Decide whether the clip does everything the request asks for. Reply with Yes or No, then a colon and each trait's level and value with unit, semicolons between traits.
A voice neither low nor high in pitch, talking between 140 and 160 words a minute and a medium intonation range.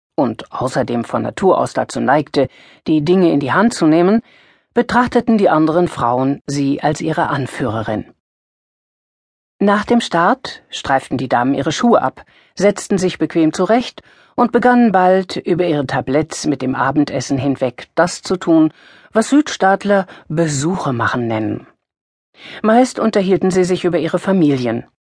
No: medium, 170 Hz; average, 145 wpm; wide, 6.0 semitones